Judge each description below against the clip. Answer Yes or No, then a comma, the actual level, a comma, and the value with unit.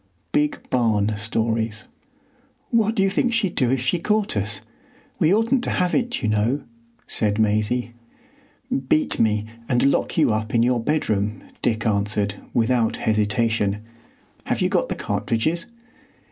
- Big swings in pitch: Yes, wide, 6.3 semitones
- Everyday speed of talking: Yes, average, 145 wpm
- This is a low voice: Yes, low, 115 Hz